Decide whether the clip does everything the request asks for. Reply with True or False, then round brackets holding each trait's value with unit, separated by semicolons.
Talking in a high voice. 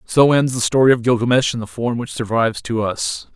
False (120 Hz)